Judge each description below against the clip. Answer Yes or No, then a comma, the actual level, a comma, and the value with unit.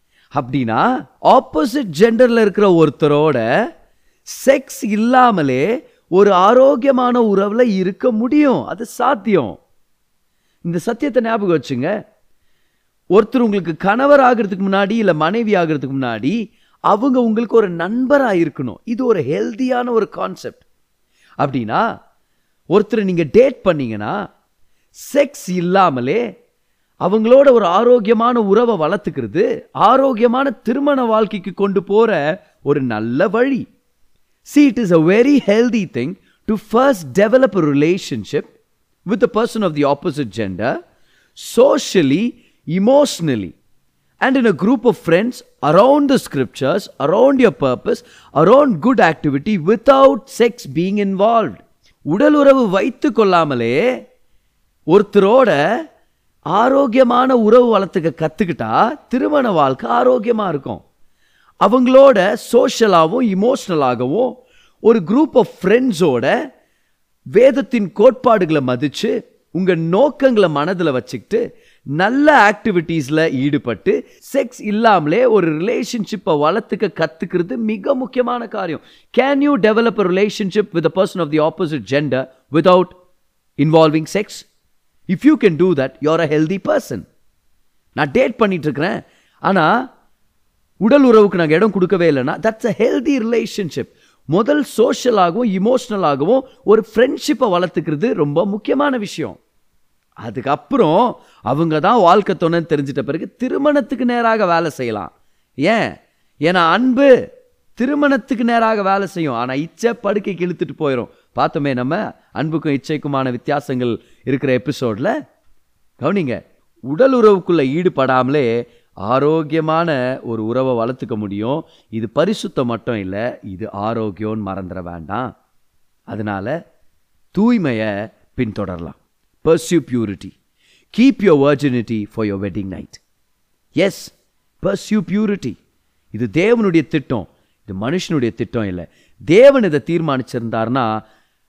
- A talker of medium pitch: No, high, 195 Hz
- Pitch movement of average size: No, wide, 8.6 semitones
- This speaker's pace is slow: No, average, 105 wpm